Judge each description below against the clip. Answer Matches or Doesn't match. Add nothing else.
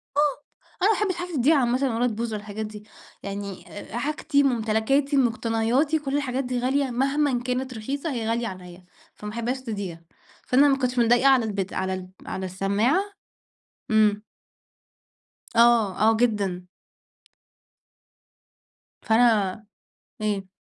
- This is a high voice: Matches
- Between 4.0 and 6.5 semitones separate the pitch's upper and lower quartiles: Matches